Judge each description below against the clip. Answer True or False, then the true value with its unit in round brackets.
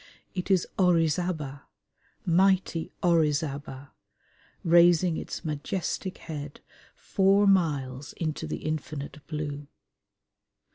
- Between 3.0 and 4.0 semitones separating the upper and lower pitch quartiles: True (3.6 semitones)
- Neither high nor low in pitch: True (160 Hz)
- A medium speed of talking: False (85 wpm)